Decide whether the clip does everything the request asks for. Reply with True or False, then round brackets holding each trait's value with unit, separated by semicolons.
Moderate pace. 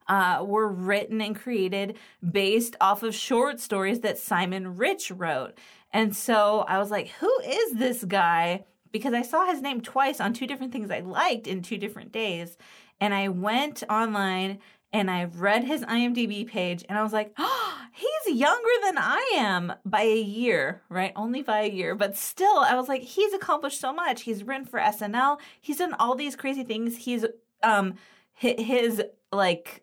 True (180 wpm)